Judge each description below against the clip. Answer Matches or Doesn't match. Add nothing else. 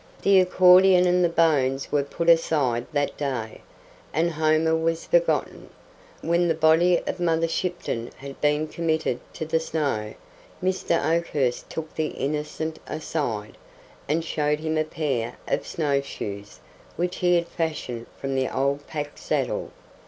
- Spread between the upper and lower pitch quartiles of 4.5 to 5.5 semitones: Doesn't match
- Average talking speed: Matches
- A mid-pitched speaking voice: Matches